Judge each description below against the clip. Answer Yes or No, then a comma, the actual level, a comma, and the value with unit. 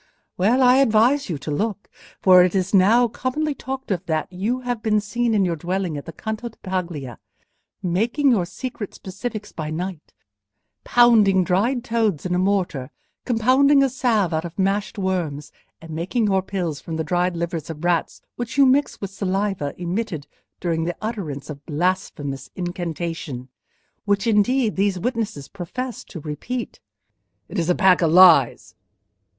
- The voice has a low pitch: No, high, 190 Hz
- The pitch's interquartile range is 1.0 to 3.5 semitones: No, average, 5.2 semitones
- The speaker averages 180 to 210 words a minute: No, average, 165 wpm